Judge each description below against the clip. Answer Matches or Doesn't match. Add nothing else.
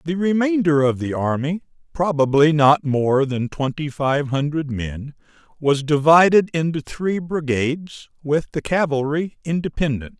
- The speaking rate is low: Matches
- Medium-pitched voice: Matches